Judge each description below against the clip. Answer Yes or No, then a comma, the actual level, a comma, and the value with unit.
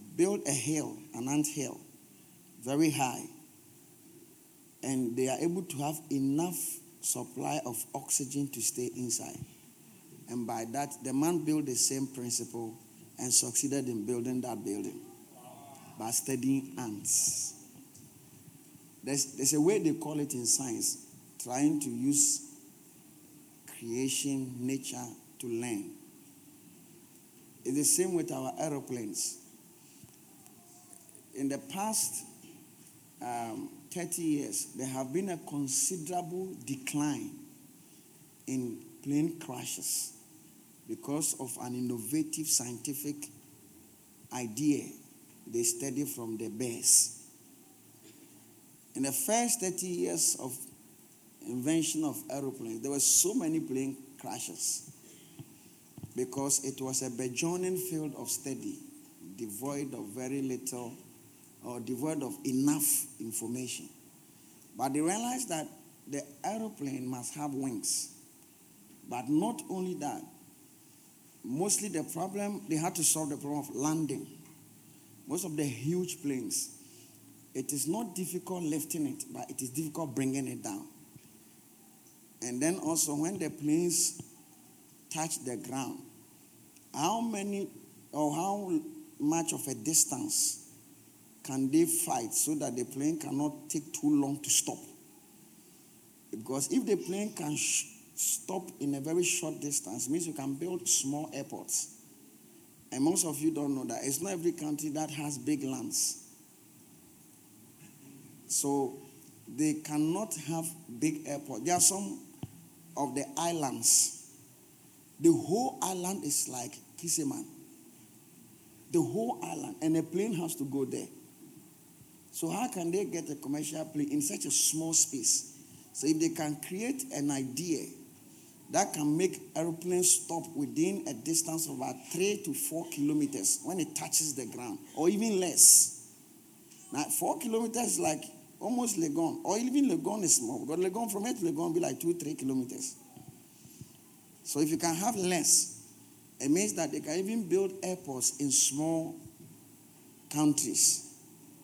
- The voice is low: No, medium, 155 Hz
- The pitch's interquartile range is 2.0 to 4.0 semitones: No, average, 5.3 semitones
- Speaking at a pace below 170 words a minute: Yes, slow, 135 wpm